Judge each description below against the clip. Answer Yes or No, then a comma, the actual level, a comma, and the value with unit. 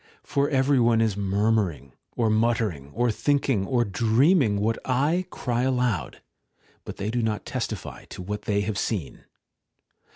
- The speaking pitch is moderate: No, low, 115 Hz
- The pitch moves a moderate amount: Yes, average, 3.6 semitones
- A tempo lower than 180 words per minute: Yes, average, 150 wpm